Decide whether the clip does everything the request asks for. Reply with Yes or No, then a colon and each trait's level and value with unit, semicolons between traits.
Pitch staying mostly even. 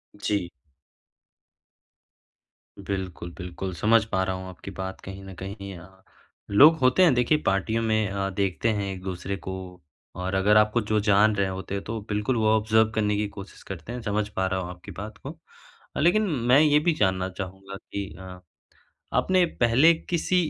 No: average, 3.1 semitones